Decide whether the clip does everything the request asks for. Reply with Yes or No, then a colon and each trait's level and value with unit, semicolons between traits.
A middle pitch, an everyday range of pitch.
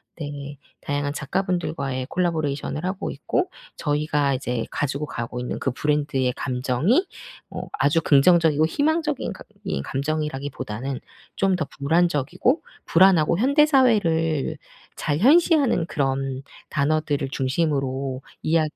Yes: medium, 150 Hz; average, 4.6 semitones